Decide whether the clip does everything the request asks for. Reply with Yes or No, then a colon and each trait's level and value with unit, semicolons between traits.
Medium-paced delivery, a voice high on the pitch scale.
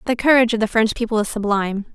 No: fast, 245 wpm; high, 225 Hz